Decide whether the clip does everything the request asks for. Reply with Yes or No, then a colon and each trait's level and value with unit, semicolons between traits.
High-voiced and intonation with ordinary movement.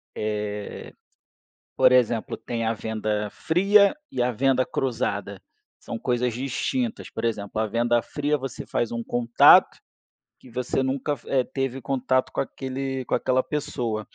No: low, 125 Hz; average, 3.1 semitones